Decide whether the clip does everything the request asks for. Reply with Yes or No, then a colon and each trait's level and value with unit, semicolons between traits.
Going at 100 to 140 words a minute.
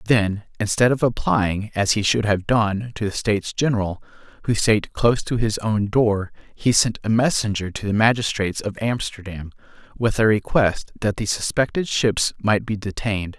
No: average, 175 wpm